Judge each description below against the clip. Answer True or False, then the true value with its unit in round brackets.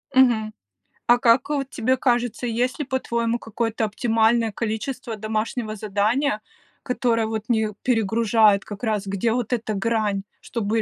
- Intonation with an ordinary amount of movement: False (2.1 semitones)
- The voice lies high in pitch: True (225 Hz)